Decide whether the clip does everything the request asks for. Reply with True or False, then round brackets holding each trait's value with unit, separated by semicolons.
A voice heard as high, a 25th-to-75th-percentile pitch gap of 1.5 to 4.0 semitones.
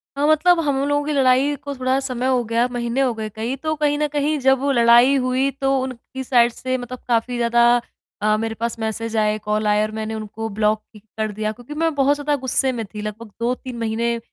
True (245 Hz; 3.4 semitones)